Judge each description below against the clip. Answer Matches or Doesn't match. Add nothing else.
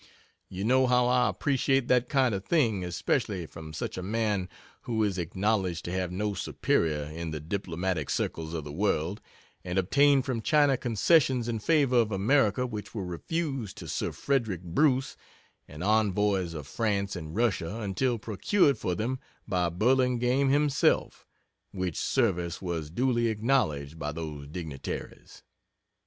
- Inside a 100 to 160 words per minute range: Matches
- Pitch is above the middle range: Doesn't match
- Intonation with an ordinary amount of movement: Doesn't match